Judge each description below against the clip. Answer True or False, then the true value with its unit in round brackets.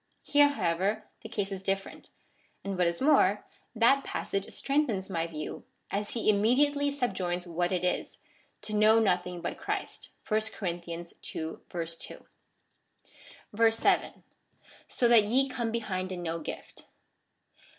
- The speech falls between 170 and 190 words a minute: False (135 wpm)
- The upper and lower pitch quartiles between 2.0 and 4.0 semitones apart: False (4.6 semitones)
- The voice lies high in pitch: True (200 Hz)